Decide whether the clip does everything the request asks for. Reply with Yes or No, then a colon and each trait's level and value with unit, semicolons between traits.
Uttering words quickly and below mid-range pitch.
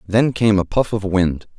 Yes: fast, 230 wpm; low, 100 Hz